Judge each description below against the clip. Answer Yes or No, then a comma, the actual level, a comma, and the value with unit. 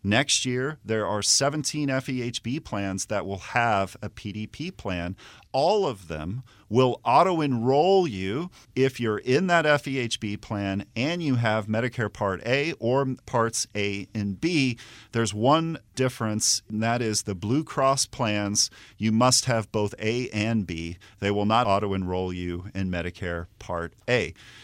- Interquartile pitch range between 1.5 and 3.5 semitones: No, average, 4.3 semitones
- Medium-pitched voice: No, low, 110 Hz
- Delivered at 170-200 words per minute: No, average, 155 wpm